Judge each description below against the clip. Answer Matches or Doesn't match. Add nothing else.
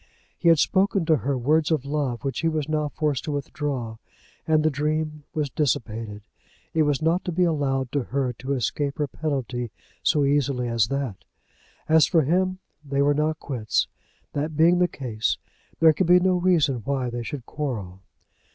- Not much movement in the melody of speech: Doesn't match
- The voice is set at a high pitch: Doesn't match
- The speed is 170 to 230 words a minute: Matches